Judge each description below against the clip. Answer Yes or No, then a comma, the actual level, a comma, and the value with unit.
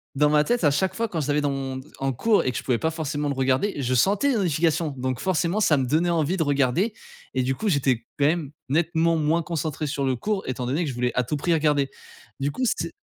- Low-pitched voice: No, medium, 150 Hz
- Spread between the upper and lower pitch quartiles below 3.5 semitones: No, average, 4.1 semitones